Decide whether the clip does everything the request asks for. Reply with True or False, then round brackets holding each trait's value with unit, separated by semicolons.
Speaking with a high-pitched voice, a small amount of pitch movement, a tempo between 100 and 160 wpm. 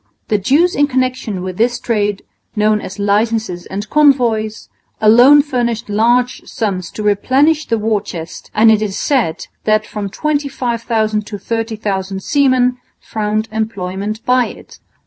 False (220 Hz; 3.3 semitones; 140 wpm)